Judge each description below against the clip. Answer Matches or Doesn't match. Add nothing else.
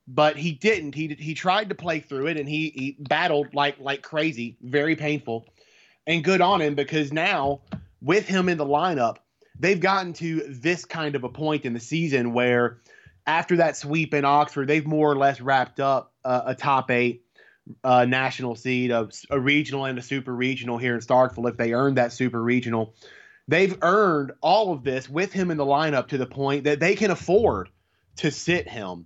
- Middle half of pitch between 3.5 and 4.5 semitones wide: Matches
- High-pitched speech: Doesn't match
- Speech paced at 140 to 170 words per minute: Doesn't match